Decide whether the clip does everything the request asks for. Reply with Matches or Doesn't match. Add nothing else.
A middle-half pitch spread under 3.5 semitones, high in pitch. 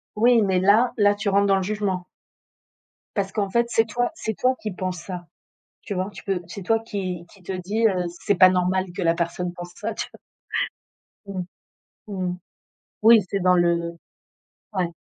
Matches